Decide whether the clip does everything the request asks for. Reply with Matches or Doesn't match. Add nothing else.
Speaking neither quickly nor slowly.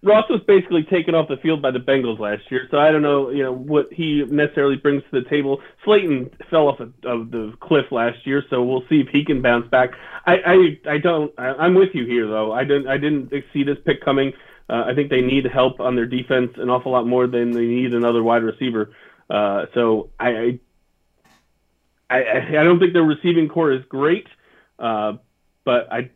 Doesn't match